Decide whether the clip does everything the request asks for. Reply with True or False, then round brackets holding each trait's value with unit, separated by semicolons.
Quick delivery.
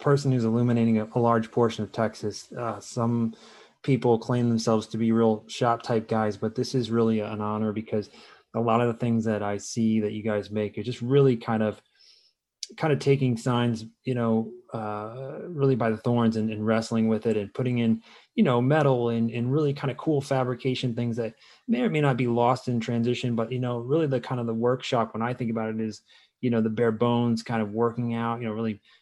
True (225 wpm)